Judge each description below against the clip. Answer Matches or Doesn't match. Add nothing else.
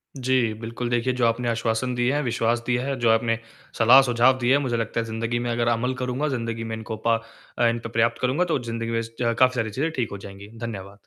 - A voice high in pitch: Doesn't match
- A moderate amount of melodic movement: Doesn't match